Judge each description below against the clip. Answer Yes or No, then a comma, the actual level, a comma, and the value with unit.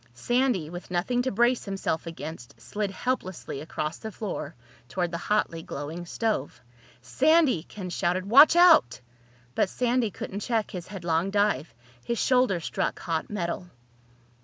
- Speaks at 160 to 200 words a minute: No, average, 140 wpm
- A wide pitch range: Yes, wide, 5.9 semitones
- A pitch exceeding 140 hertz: Yes, high, 190 Hz